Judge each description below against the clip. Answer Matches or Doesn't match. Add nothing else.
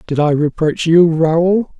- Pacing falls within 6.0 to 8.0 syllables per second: Doesn't match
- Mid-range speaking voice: Matches